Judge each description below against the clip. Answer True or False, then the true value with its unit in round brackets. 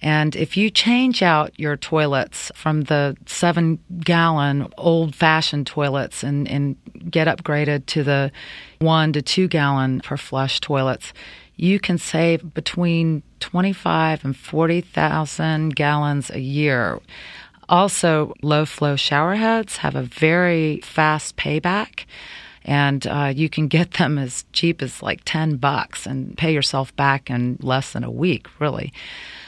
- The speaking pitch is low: False (155 Hz)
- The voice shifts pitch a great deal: False (2.9 semitones)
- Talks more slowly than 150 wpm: True (135 wpm)